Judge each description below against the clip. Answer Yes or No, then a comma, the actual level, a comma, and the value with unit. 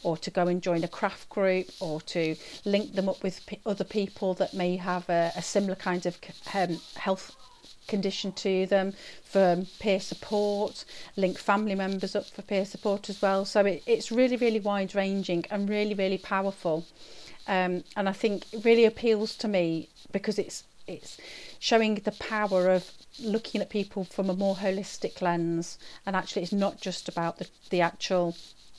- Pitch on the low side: No, high, 195 Hz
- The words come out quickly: No, average, 180 wpm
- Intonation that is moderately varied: No, narrow, 2.3 semitones